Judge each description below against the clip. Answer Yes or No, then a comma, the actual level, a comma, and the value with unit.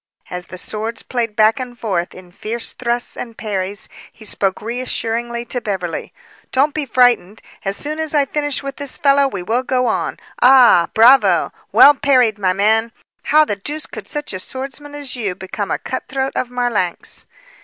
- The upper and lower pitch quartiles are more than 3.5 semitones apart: Yes, average, 4.7 semitones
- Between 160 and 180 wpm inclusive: Yes, average, 175 wpm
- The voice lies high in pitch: Yes, high, 235 Hz